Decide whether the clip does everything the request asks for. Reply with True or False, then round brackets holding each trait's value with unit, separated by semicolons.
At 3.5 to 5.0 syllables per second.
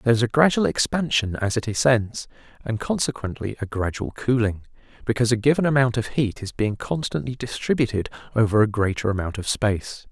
False (5.9 syllables/s)